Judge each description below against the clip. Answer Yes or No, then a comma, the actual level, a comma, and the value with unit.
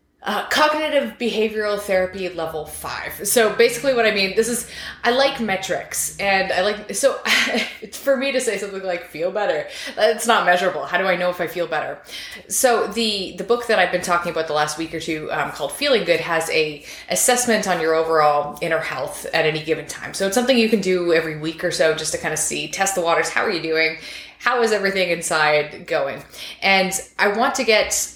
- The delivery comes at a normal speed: No, fast, 215 wpm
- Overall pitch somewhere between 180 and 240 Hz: Yes, high, 190 Hz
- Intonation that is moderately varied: No, wide, 5.9 semitones